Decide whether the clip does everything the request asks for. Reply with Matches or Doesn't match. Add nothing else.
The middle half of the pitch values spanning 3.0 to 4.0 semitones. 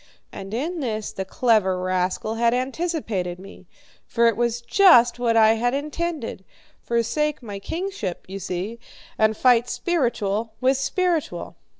Doesn't match